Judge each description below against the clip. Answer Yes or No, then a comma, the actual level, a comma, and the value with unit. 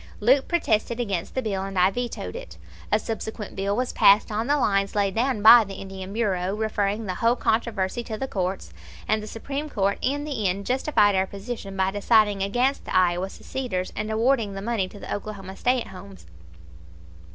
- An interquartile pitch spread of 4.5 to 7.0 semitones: No, average, 3.5 semitones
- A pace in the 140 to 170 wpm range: No, average, 195 wpm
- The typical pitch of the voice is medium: No, high, 210 Hz